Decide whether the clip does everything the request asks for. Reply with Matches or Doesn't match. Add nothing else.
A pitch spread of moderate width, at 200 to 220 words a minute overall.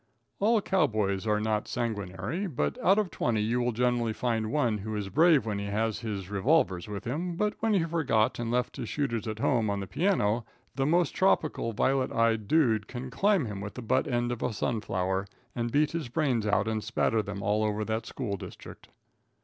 Matches